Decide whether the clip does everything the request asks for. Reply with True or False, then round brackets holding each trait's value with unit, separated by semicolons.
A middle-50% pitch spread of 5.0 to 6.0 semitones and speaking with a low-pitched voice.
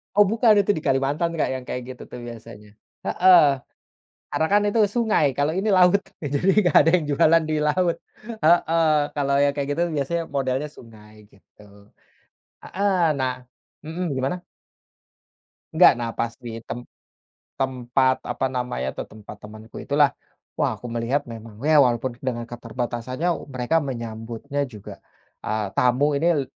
True (5.3 semitones; 130 Hz)